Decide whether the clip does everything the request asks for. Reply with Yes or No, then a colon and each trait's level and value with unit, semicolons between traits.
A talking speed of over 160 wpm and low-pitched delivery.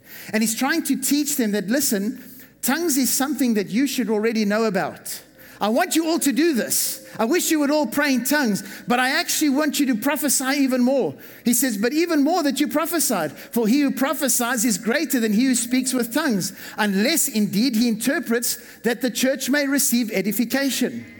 No: average, 200 wpm; very high, 255 Hz